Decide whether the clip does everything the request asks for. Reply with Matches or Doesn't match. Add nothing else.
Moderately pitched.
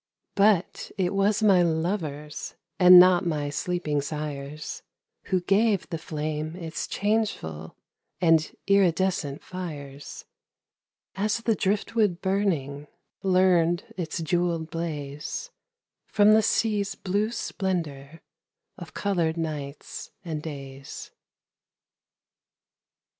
Matches